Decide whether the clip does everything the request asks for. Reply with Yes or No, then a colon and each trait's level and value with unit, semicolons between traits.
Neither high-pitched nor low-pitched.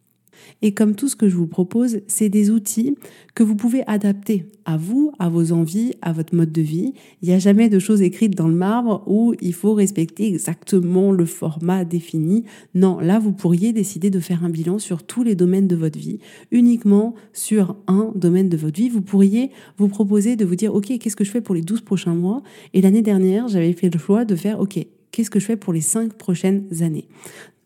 No: high, 200 Hz